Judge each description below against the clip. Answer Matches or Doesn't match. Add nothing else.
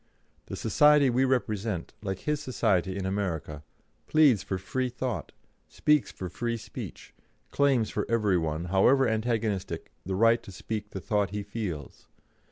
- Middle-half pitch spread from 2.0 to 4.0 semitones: Doesn't match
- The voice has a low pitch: Matches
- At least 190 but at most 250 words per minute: Doesn't match